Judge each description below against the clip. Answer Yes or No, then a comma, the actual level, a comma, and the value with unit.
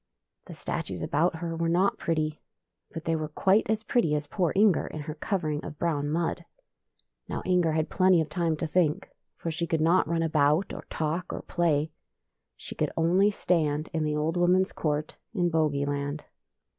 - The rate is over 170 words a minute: Yes, average, 185 wpm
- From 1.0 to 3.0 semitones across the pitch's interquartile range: Yes, narrow, 2.5 semitones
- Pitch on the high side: No, medium, 160 Hz